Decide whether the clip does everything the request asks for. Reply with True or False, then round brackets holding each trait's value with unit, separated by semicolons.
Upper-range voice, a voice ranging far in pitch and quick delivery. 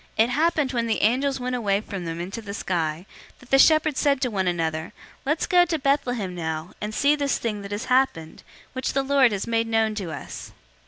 True (230 Hz; 6.1 semitones; 220 wpm)